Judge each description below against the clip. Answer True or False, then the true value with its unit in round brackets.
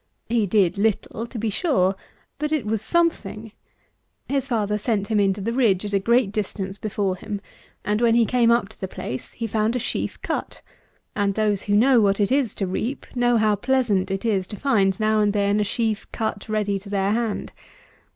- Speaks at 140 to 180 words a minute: False (205 wpm)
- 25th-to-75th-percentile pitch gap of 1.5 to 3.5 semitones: True (2.7 semitones)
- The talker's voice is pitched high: True (215 Hz)